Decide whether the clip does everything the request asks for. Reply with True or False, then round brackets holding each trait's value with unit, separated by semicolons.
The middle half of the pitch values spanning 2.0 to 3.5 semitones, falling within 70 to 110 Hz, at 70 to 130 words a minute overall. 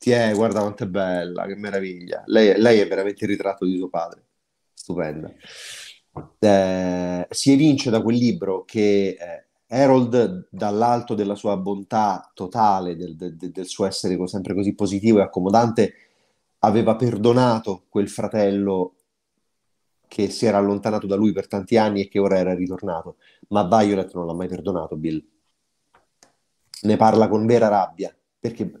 False (2.8 semitones; 100 Hz; 150 wpm)